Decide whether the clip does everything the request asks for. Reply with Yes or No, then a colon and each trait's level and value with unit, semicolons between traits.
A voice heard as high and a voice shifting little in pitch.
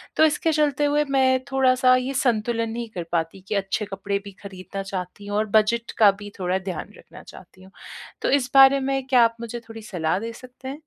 No: high, 230 Hz; average, 4.9 semitones